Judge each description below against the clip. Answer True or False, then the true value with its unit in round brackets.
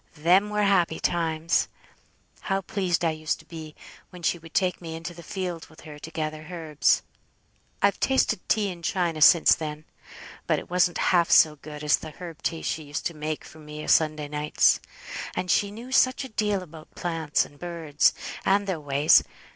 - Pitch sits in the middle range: True (165 Hz)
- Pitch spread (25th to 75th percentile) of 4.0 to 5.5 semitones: False (2.9 semitones)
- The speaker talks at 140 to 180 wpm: False (190 wpm)